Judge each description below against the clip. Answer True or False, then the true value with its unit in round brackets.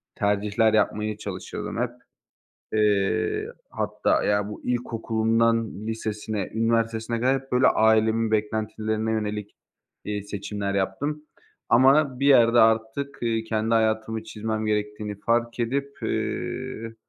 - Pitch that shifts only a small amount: True (1.5 semitones)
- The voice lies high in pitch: False (110 Hz)